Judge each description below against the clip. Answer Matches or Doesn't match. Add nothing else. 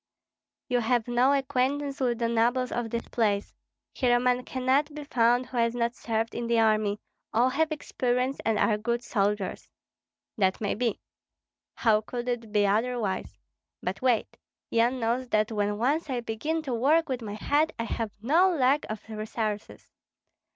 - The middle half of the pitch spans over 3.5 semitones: Doesn't match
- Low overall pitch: Doesn't match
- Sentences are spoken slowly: Doesn't match